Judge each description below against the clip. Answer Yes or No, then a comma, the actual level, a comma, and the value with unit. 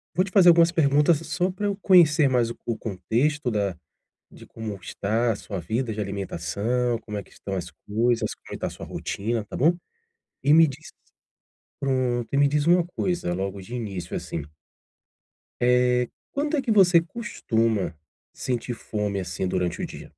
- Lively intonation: Yes, wide, 7.7 semitones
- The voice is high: No, low, 120 Hz